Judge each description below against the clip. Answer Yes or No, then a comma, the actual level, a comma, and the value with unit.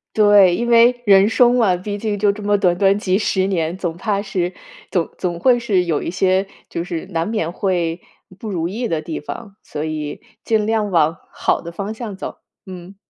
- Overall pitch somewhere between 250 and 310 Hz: No, high, 195 Hz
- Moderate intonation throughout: Yes, average, 3.4 semitones